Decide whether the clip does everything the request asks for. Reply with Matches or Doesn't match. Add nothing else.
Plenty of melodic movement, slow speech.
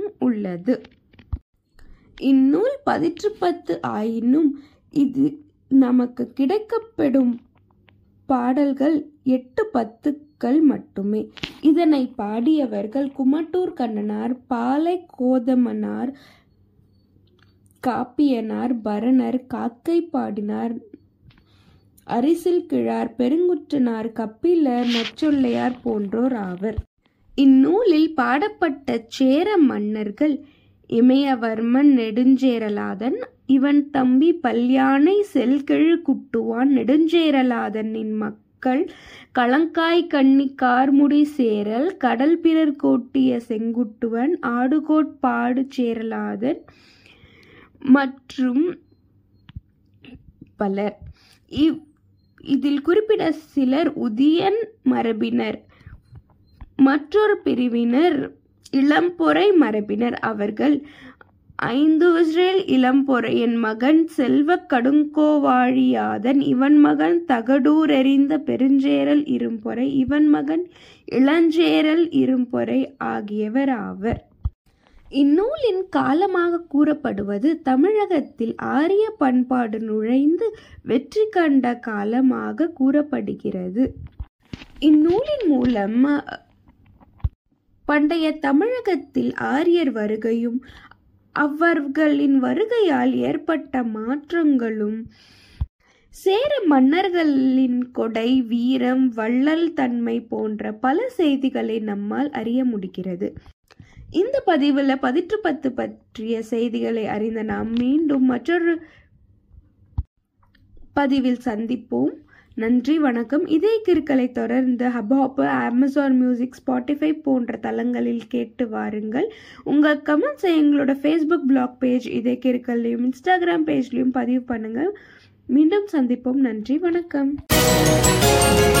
Doesn't match